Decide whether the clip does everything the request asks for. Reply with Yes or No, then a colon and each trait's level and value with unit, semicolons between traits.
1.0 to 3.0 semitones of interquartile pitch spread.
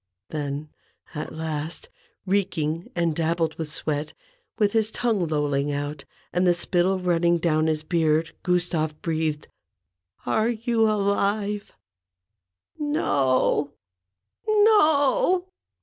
No: average, 5.1 semitones